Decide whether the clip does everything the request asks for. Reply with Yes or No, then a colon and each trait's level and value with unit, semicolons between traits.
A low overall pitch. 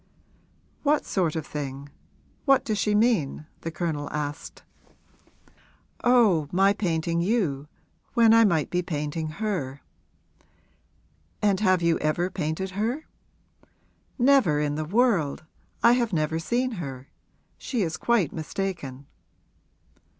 No: medium, 175 Hz